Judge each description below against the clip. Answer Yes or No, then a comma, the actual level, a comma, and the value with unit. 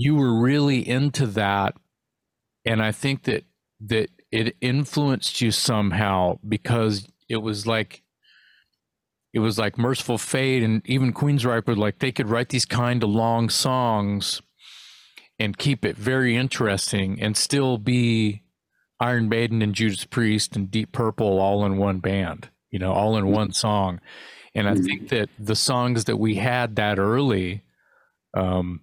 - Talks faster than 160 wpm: No, average, 155 wpm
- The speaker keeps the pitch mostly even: No, average, 3.4 semitones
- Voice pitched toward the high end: No, low, 110 Hz